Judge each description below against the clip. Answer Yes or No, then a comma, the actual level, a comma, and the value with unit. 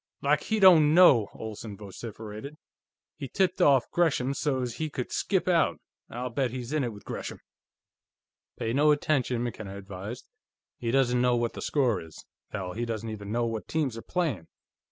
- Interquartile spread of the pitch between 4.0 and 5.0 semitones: Yes, average, 4.7 semitones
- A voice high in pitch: No, low, 120 Hz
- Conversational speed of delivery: Yes, average, 175 wpm